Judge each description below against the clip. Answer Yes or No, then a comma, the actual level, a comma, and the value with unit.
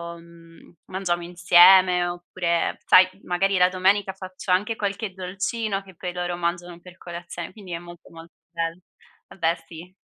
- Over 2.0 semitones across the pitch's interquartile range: No, narrow, 1.7 semitones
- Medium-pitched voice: Yes, medium, 180 Hz